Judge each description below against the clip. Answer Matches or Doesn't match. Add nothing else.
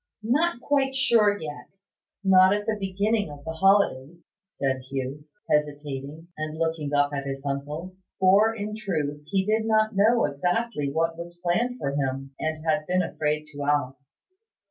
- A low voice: Doesn't match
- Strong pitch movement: Matches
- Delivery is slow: Doesn't match